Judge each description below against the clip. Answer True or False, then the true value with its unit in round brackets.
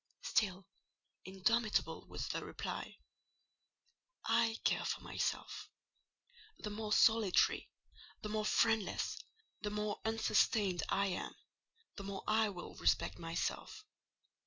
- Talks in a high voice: True (210 Hz)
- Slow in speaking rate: True (105 wpm)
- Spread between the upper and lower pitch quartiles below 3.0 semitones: True (2.4 semitones)